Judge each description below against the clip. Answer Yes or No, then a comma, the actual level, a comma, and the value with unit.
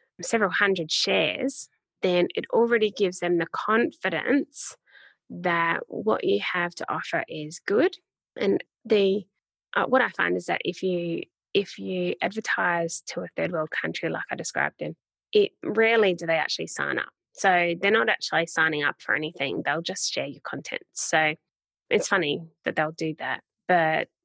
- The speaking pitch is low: No, medium, 175 Hz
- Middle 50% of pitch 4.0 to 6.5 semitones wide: Yes, average, 5.0 semitones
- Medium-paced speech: Yes, average, 170 wpm